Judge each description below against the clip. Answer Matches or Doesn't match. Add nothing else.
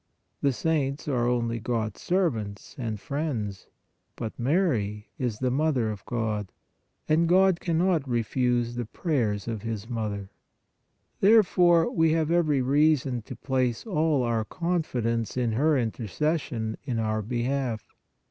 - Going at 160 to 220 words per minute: Doesn't match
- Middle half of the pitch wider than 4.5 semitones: Matches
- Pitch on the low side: Matches